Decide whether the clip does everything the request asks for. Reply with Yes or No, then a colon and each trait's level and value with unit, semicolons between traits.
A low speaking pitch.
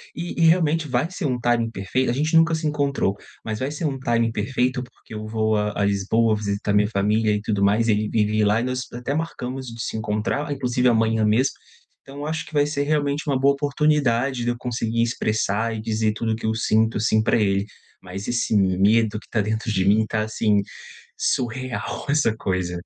Yes: low, 115 Hz